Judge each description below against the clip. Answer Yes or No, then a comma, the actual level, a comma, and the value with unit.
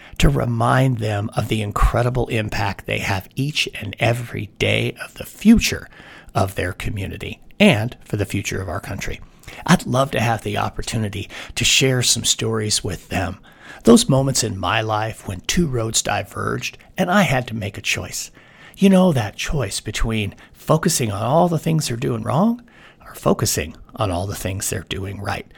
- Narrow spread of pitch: No, average, 4.1 semitones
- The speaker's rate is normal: Yes, average, 180 wpm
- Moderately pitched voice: No, low, 115 Hz